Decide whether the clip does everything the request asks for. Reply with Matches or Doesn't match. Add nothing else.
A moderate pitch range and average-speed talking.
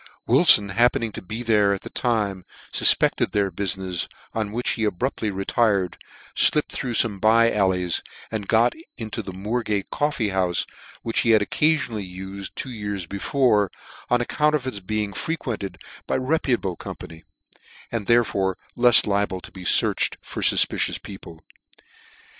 Matches